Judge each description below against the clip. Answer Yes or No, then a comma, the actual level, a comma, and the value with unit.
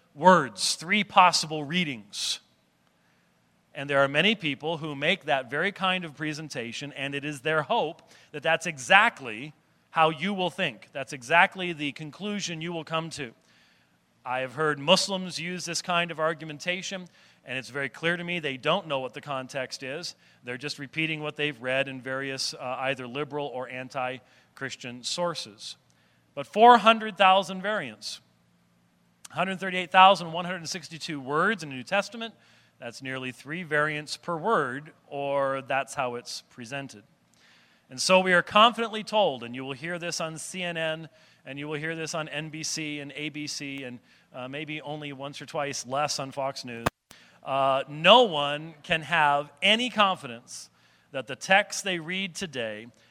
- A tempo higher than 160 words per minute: No, average, 155 wpm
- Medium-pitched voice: Yes, medium, 150 Hz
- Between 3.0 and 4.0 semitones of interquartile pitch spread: No, average, 4.7 semitones